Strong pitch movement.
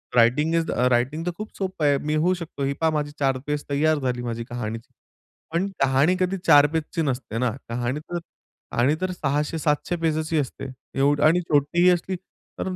No: average, 3.7 semitones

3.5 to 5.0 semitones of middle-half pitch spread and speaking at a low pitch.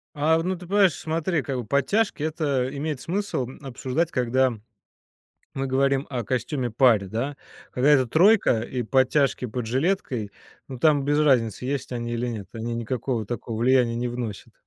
Yes: average, 3.8 semitones; low, 130 Hz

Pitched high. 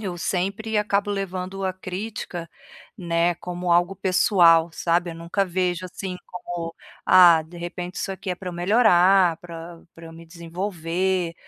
No: medium, 180 Hz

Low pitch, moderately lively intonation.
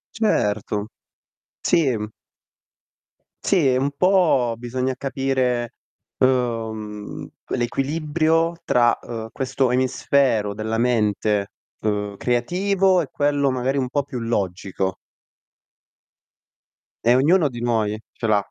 Yes: low, 125 Hz; average, 4.1 semitones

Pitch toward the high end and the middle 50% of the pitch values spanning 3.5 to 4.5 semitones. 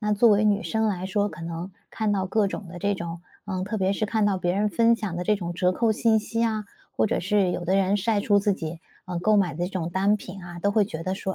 No: high, 195 Hz; average, 2.8 semitones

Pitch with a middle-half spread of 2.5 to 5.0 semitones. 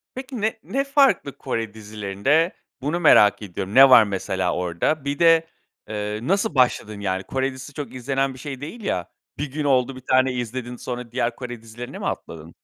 No: wide, 5.4 semitones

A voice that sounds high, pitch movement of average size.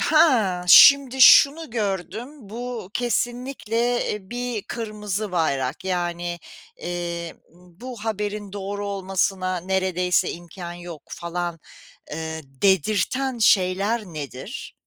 Yes: high, 195 Hz; average, 4.9 semitones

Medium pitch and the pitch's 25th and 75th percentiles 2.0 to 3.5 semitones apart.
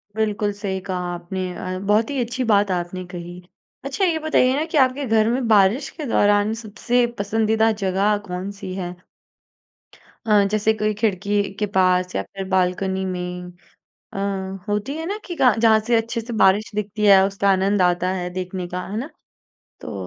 No: high, 205 Hz; average, 3.1 semitones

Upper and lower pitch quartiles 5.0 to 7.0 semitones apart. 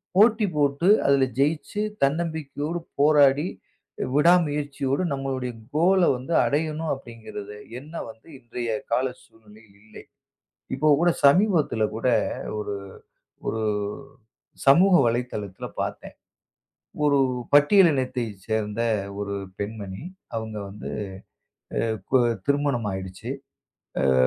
Yes: wide, 5.5 semitones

